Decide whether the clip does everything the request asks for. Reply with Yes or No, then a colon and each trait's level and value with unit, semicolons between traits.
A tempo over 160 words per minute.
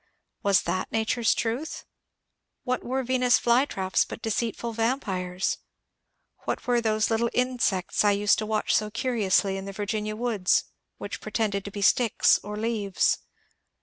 No: average, 145 wpm